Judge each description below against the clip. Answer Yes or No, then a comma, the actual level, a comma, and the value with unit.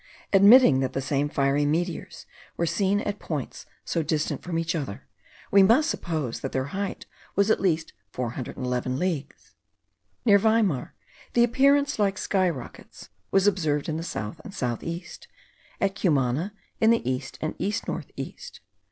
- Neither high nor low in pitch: Yes, medium, 170 Hz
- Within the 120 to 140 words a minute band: No, average, 160 wpm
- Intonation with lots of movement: Yes, wide, 6.4 semitones